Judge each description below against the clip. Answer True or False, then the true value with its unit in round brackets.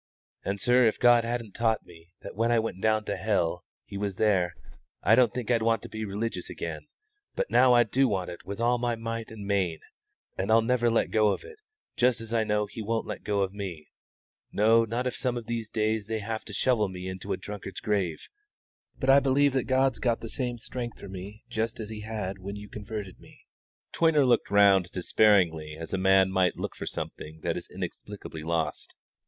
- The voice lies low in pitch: True (110 Hz)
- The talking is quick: True (215 wpm)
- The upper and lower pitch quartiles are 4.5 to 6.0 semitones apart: False (3.4 semitones)